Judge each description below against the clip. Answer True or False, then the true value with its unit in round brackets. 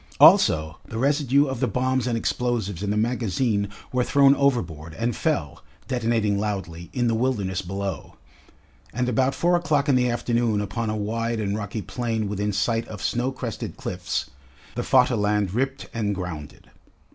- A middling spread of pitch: True (3.7 semitones)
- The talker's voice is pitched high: False (115 Hz)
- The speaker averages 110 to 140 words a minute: False (160 wpm)